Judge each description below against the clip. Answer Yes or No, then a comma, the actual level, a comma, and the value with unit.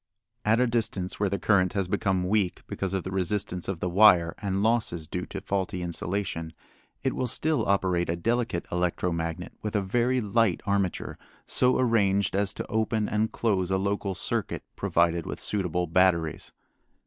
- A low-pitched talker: Yes, very low, 95 Hz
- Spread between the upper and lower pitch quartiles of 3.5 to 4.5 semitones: No, average, 3.1 semitones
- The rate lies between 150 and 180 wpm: Yes, average, 170 wpm